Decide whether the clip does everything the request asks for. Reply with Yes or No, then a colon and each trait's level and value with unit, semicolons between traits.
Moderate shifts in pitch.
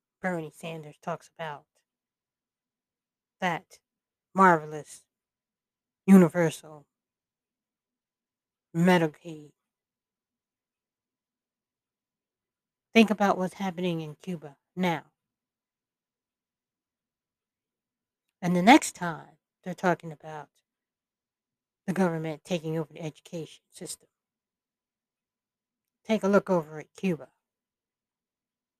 Yes: average, 3.2 semitones